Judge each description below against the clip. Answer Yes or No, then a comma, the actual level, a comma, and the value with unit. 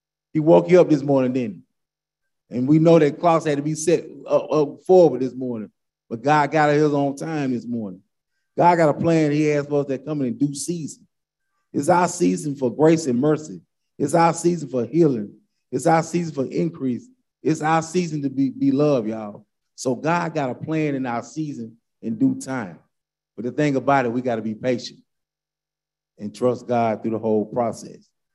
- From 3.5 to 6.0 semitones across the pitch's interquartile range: Yes, average, 3.9 semitones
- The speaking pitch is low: No, medium, 145 Hz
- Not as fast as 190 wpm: No, average, 195 wpm